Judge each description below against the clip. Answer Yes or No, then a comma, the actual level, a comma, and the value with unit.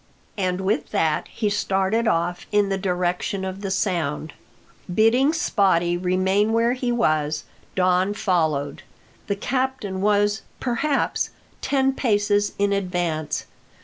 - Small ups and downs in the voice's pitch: No, average, 3.5 semitones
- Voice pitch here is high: Yes, high, 195 Hz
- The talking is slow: Yes, slow, 120 wpm